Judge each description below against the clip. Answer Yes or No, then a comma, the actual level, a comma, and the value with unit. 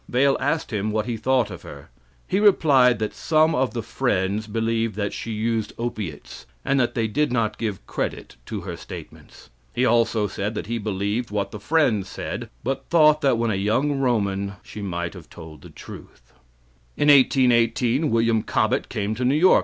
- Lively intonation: No, average, 4.1 semitones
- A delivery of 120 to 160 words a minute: No, average, 185 wpm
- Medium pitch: No, low, 115 Hz